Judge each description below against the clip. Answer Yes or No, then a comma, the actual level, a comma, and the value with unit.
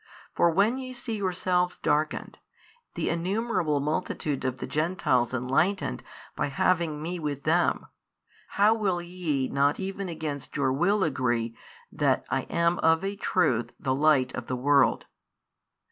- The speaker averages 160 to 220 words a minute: No, average, 145 wpm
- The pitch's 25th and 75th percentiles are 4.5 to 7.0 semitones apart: Yes, average, 5.0 semitones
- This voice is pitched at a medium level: Yes, medium, 160 Hz